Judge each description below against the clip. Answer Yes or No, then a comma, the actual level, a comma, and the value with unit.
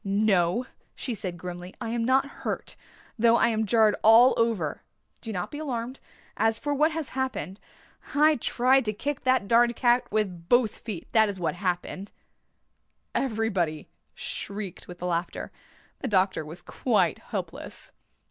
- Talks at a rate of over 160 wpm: No, average, 150 wpm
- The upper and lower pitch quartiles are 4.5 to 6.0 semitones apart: Yes, average, 4.9 semitones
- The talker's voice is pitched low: No, high, 220 Hz